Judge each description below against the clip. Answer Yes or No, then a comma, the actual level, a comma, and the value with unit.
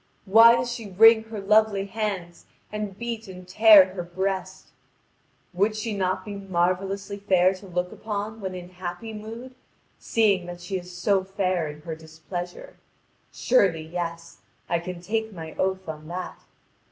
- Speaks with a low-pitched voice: No, high, 190 Hz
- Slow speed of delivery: No, average, 155 wpm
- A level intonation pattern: No, average, 3.2 semitones